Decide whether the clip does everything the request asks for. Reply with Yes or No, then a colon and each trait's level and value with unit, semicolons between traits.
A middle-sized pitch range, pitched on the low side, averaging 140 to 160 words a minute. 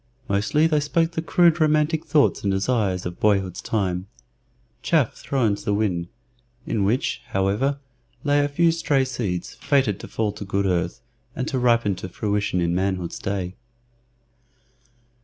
No: wide, 7.0 semitones; low, 105 Hz; average, 155 wpm